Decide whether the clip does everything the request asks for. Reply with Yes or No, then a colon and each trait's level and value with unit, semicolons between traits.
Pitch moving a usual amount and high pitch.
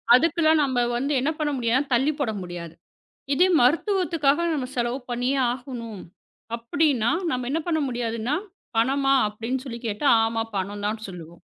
Yes: average, 4.1 semitones; very high, 250 Hz